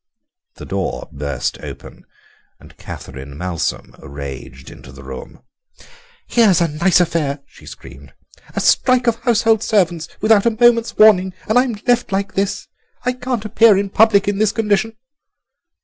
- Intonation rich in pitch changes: Yes, wide, 6.9 semitones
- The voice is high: Yes, high, 200 Hz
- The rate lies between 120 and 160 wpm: Yes, average, 150 wpm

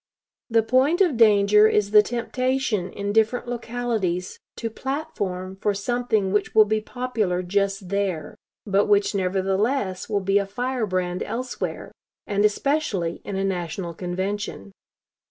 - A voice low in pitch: No, high, 205 Hz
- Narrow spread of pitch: No, average, 3.7 semitones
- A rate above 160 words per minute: No, slow, 135 wpm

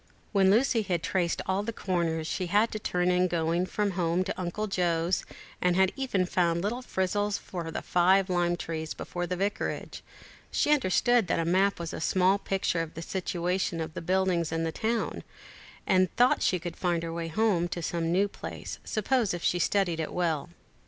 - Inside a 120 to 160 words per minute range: No, average, 190 wpm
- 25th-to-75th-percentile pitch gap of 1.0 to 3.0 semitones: Yes, narrow, 2.6 semitones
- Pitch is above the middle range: No, medium, 180 Hz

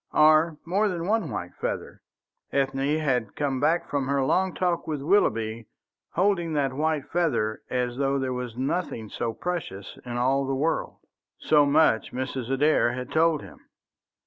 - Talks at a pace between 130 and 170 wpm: Yes, average, 160 wpm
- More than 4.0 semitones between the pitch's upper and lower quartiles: Yes, average, 4.4 semitones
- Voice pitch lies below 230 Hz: Yes, medium, 140 Hz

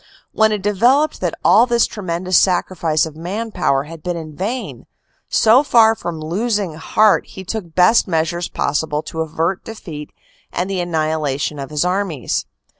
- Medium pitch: Yes, medium, 175 Hz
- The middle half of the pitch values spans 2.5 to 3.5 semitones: No, average, 5.0 semitones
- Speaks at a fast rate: No, average, 160 wpm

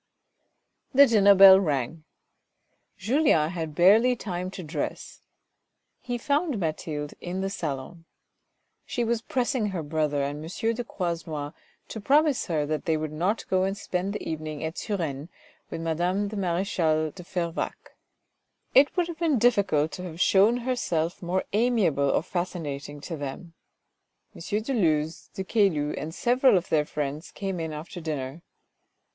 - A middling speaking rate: Yes, average, 150 wpm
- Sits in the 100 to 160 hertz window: No, medium, 175 Hz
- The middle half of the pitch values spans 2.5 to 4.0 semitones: No, average, 5.0 semitones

